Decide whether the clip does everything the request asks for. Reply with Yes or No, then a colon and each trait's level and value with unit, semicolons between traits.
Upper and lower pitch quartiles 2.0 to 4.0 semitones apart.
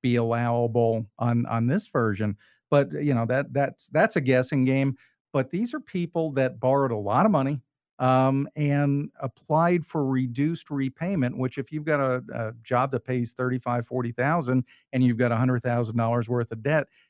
Yes: average, 2.9 semitones